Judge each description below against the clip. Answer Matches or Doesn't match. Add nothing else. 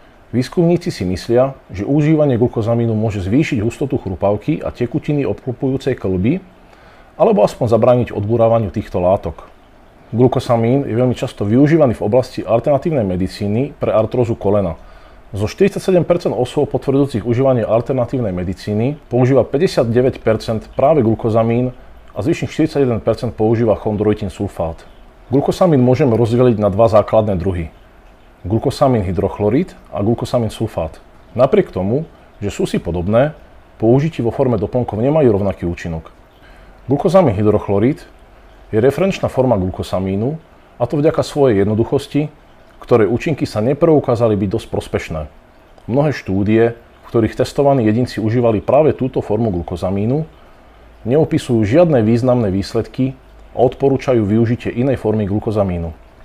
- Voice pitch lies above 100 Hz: Matches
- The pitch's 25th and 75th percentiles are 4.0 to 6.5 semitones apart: Matches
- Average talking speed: Matches